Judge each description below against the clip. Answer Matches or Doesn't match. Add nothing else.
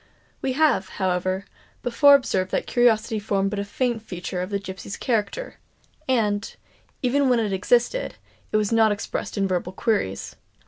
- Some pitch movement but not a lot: Matches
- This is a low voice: Doesn't match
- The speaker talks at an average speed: Matches